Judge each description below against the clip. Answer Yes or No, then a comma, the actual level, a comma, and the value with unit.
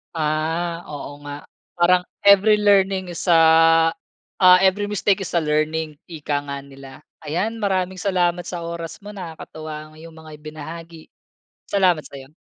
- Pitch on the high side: No, medium, 165 Hz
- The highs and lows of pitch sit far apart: No, average, 3.2 semitones